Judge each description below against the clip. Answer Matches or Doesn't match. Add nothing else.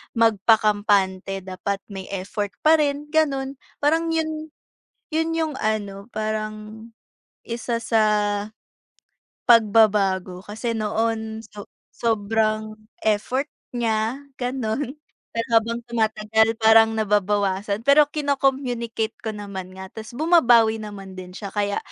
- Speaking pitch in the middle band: Doesn't match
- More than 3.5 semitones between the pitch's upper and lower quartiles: Doesn't match